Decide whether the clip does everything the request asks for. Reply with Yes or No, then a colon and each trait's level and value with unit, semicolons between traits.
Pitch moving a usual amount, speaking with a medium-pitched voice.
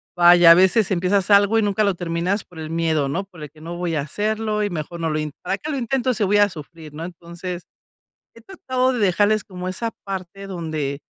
Yes: average, 3.8 semitones; medium, 180 Hz